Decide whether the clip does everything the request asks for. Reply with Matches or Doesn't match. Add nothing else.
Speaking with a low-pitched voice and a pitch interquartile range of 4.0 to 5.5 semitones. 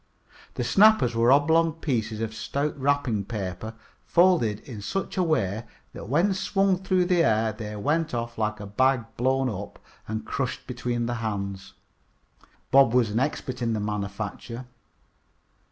Matches